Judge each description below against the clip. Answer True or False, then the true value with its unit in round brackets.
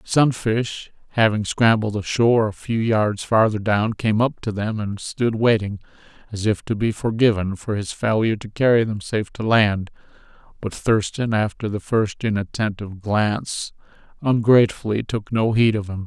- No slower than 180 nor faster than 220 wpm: False (160 wpm)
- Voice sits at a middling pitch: False (110 Hz)